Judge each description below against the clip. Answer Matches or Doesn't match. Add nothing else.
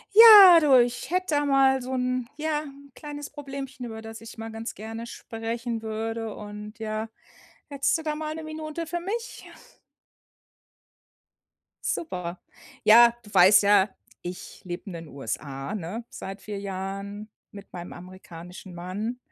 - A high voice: Matches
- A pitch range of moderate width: Doesn't match